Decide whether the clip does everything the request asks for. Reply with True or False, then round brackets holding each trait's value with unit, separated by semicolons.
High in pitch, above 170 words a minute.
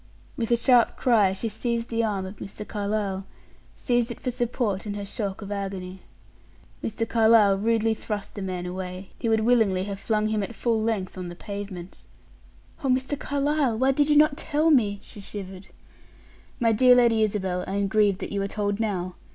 True (215 Hz; 190 wpm)